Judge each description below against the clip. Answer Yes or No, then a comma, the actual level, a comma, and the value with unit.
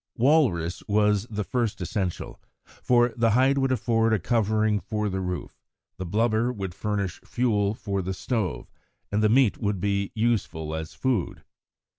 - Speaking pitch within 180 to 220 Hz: No, low, 105 Hz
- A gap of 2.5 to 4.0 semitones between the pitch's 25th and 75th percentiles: Yes, average, 3.4 semitones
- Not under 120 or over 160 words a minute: Yes, average, 155 wpm